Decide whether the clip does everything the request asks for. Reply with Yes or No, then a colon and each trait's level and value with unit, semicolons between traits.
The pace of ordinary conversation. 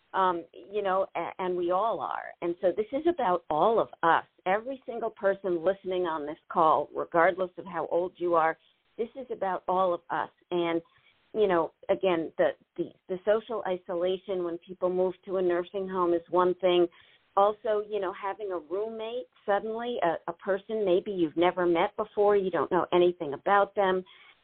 Yes: average, 180 wpm